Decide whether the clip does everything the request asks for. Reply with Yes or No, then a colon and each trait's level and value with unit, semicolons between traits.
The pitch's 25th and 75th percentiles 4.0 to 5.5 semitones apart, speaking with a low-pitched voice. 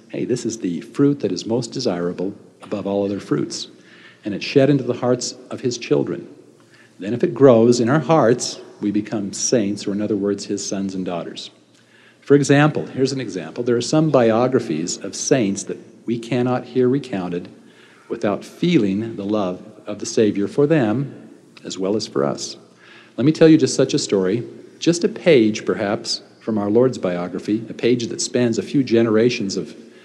Yes: average, 4.3 semitones; low, 115 Hz